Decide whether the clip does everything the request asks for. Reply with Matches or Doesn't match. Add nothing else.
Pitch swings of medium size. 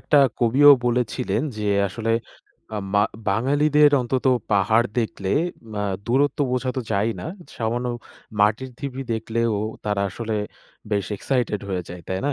Matches